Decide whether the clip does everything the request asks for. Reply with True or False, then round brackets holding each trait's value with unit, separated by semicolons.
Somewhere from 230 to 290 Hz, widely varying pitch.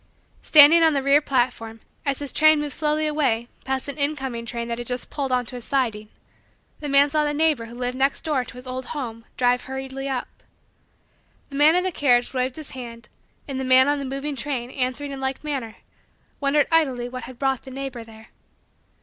False (265 Hz; 2.8 semitones)